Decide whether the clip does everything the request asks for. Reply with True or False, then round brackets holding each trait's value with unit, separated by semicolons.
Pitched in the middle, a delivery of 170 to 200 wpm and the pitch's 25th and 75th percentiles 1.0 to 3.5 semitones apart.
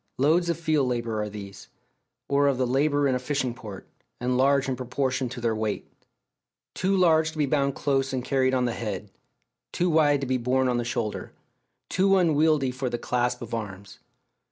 False (130 Hz; 195 wpm; 3.2 semitones)